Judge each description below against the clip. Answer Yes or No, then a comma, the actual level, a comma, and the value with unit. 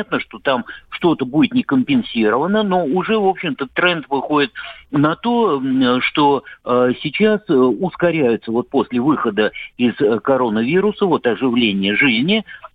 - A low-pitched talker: No, medium, 165 Hz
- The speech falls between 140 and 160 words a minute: No, average, 115 wpm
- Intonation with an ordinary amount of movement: No, wide, 8.5 semitones